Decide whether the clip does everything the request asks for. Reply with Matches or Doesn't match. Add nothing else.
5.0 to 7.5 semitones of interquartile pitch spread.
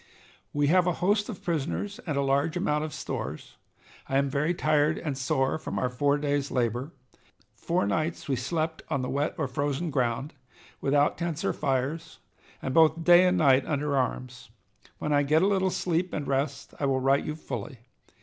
Doesn't match